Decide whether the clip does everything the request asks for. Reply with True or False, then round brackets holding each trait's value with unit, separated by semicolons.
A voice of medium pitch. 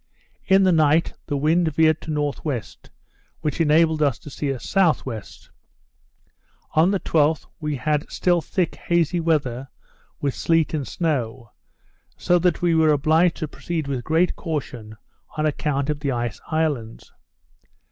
True (155 Hz)